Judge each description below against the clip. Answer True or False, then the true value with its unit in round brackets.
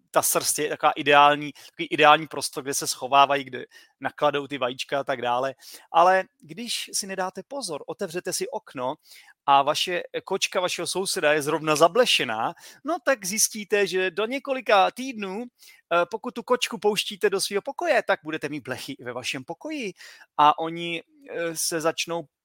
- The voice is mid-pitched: True (170 Hz)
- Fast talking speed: False (155 wpm)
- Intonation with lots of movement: True (5.8 semitones)